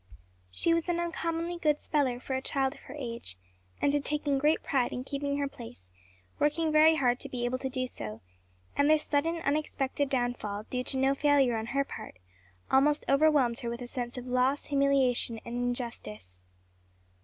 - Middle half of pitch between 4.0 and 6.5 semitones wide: No, average, 3.2 semitones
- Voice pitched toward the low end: No, very high, 270 Hz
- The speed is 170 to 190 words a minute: Yes, average, 185 wpm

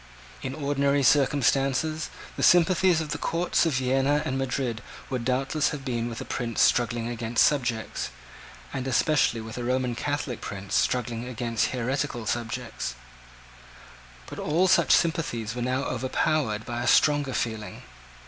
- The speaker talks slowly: No, average, 145 wpm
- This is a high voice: No, low, 130 Hz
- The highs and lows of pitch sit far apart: No, average, 3.5 semitones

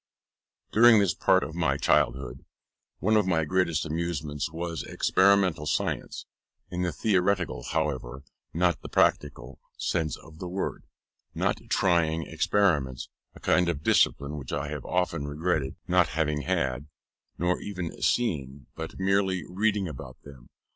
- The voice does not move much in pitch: No, average, 4.1 semitones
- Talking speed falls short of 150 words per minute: Yes, average, 140 wpm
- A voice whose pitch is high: No, very low, 80 Hz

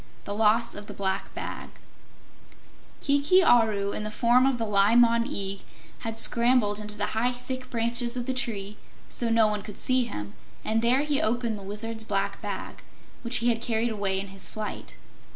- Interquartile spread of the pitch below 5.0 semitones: Yes, average, 2.7 semitones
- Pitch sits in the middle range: No, high, 225 Hz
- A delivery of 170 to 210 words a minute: Yes, average, 190 wpm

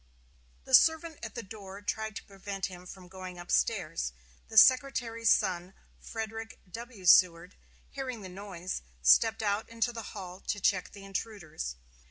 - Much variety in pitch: No, average, 3.6 semitones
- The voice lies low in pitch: No, high, 200 Hz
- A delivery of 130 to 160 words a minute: Yes, average, 155 wpm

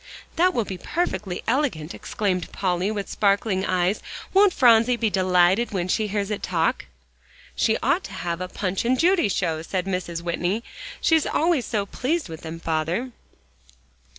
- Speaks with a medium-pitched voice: No, high, 200 Hz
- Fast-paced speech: No, average, 160 wpm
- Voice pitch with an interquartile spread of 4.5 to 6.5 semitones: Yes, average, 5.2 semitones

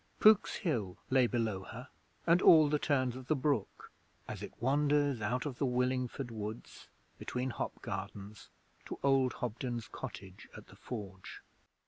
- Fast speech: No, average, 150 wpm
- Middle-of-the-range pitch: No, low, 125 Hz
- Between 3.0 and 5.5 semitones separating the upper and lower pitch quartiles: Yes, average, 4.2 semitones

